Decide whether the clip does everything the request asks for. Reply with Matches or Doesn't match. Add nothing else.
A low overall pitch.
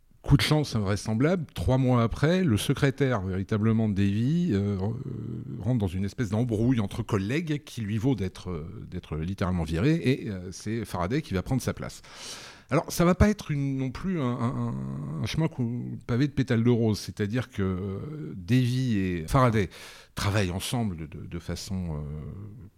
Matches